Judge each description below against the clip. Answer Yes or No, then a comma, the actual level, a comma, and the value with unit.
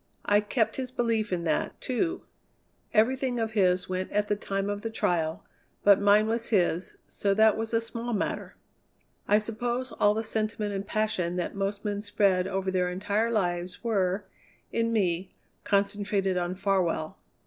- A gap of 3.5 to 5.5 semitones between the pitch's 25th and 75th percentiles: No, average, 3.0 semitones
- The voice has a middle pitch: No, high, 205 Hz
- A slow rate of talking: No, average, 165 wpm